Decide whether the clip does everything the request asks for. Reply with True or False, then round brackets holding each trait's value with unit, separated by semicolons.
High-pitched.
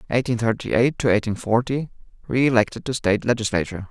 False (115 Hz)